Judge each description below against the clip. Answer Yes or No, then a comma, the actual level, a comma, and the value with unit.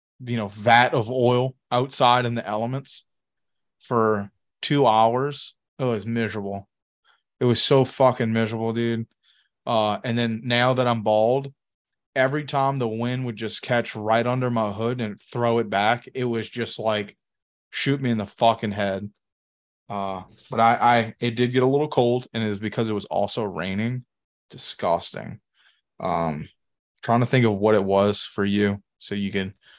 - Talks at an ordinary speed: Yes, average, 170 wpm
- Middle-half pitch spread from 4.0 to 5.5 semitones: No, average, 2.8 semitones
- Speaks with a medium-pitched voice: No, low, 115 Hz